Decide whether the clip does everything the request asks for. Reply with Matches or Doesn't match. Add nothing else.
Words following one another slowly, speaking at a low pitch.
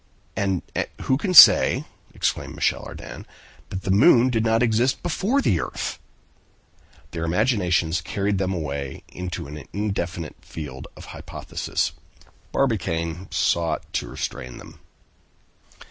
Matches